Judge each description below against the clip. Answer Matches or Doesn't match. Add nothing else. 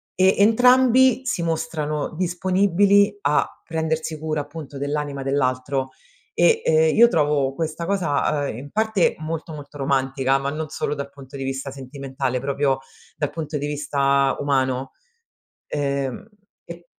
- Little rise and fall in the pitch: Doesn't match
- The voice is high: Doesn't match